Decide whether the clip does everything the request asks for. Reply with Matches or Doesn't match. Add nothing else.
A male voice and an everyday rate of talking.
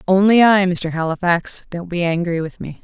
Doesn't match